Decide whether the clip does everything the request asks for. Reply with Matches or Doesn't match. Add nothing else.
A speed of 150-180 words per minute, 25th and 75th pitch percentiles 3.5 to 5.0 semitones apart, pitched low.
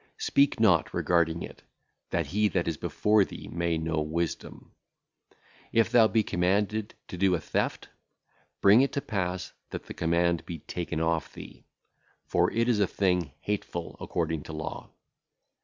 Matches